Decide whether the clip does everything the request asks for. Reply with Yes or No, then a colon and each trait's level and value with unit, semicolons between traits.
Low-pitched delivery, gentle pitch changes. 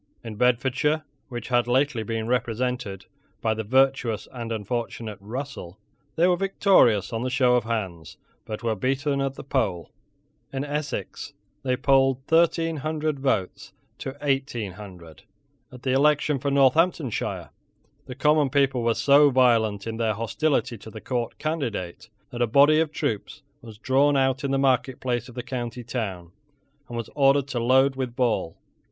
No: low, 125 Hz; average, 3.5 semitones